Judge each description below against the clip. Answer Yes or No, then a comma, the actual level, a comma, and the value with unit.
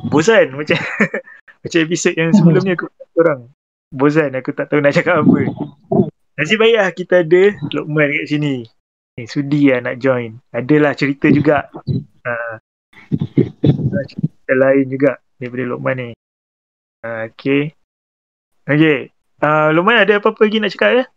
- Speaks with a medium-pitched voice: Yes, medium, 145 Hz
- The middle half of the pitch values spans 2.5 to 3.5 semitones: No, average, 5.3 semitones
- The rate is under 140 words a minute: No, average, 145 wpm